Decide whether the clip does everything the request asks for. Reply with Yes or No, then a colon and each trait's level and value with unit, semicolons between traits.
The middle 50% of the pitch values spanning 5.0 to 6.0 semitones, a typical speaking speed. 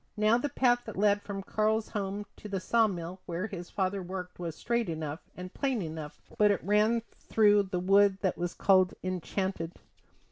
No: average, 2.8 semitones; average, 185 wpm